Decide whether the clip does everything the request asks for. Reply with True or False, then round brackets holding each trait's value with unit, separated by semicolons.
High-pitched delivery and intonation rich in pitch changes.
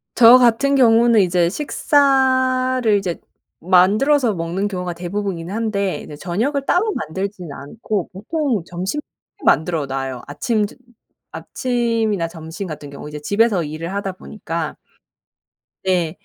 True (200 Hz; 5.9 semitones)